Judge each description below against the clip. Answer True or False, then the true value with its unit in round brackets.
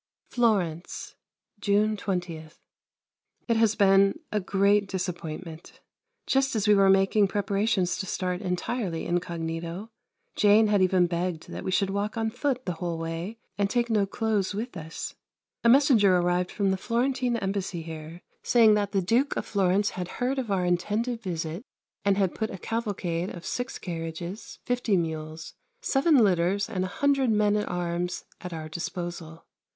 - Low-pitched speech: False (195 Hz)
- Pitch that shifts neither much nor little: True (3.8 semitones)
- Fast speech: False (160 wpm)